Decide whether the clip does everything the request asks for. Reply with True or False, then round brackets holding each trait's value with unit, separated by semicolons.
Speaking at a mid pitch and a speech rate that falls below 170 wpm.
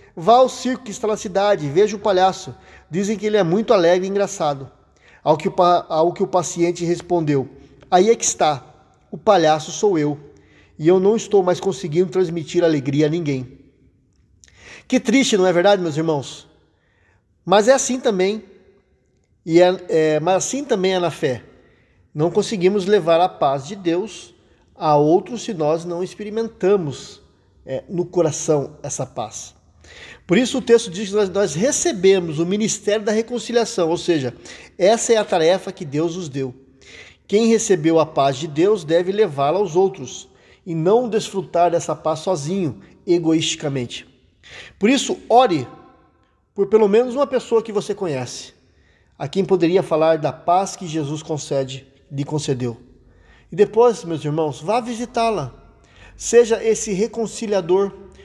True (175 Hz; 155 wpm)